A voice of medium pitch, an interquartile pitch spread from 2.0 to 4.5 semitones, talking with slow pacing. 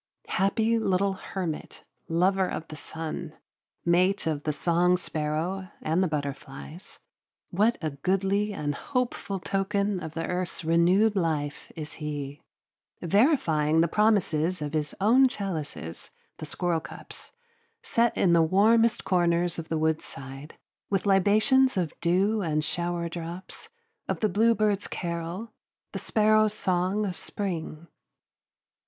Yes: medium, 180 Hz; average, 4.0 semitones; slow, 125 wpm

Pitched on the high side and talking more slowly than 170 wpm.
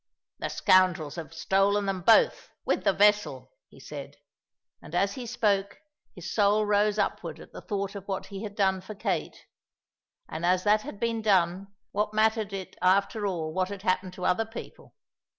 No: high, 195 Hz; average, 180 wpm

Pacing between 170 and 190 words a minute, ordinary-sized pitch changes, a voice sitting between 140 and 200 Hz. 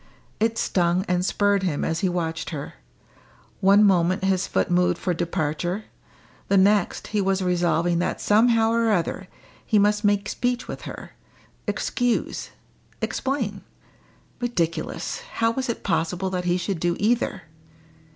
No: average, 140 wpm; average, 3.3 semitones; high, 190 Hz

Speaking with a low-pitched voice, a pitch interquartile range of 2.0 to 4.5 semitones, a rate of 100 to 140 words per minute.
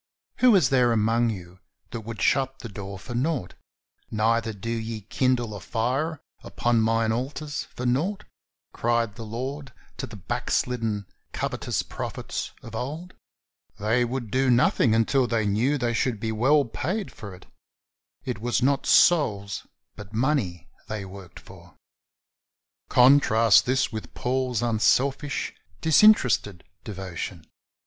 Yes: low, 115 Hz; average, 3.5 semitones; slow, 135 wpm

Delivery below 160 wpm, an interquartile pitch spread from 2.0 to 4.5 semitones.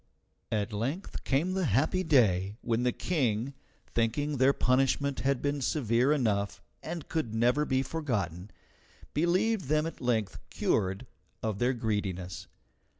No: slow, 135 wpm; wide, 5.5 semitones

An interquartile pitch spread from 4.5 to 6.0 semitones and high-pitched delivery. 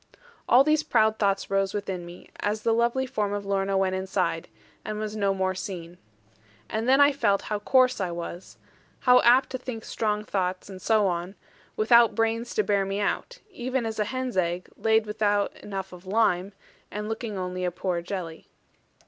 No: average, 3.2 semitones; high, 205 Hz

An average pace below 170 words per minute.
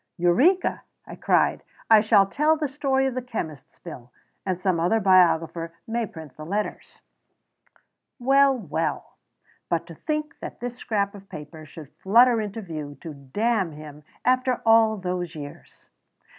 Yes: average, 150 wpm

